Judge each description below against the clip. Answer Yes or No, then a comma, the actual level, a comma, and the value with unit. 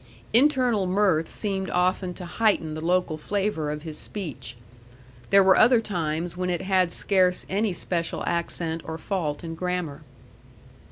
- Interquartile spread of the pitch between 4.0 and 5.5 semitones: No, average, 3.3 semitones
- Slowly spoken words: No, average, 150 wpm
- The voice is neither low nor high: Yes, medium, 180 Hz